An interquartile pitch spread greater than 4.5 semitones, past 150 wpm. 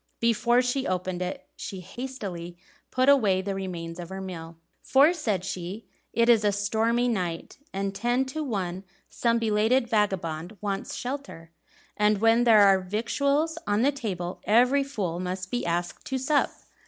Yes: average, 5.0 semitones; average, 160 wpm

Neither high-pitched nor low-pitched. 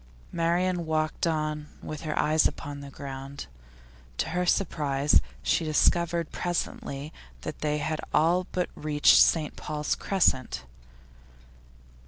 Yes: medium, 155 Hz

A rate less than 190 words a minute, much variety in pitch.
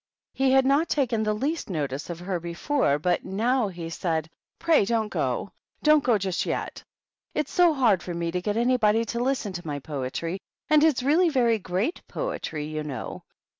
No: average, 195 wpm; wide, 7.7 semitones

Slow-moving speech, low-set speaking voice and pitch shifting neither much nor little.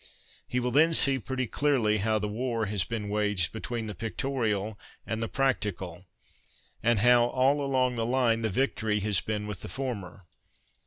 No: average, 170 wpm; low, 115 Hz; average, 3.5 semitones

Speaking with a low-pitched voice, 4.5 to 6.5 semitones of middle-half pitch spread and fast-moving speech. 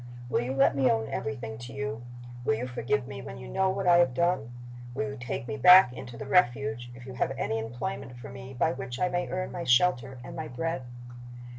Yes: low, 130 Hz; average, 5.1 semitones; fast, 230 wpm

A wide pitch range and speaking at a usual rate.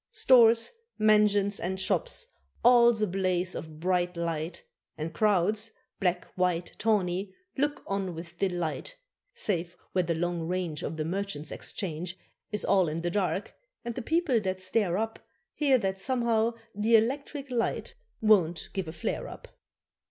No: average, 4.2 semitones; average, 150 wpm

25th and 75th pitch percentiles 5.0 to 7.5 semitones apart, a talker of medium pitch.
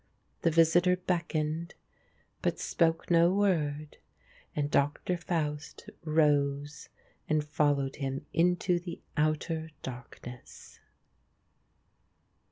No: average, 2.7 semitones; medium, 155 Hz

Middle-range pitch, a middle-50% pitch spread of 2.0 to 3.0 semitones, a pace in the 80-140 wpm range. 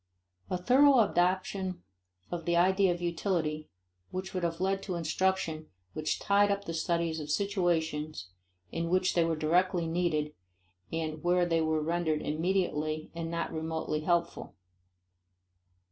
Yes: medium, 170 Hz; average, 2.7 semitones; slow, 135 wpm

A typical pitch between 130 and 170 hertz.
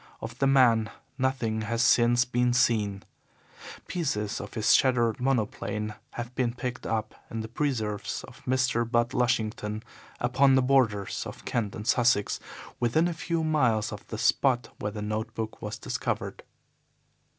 No: low, 120 Hz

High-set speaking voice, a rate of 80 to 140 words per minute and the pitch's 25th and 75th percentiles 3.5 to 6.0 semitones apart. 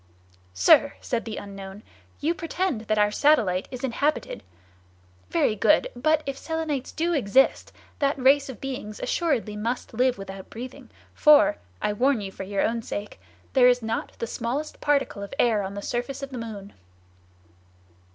No: high, 240 Hz; average, 155 wpm; average, 5.3 semitones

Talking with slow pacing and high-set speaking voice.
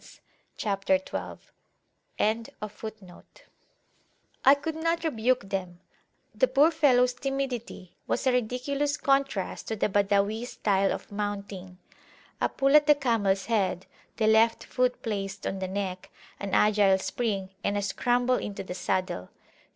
Yes: slow, 130 wpm; high, 220 Hz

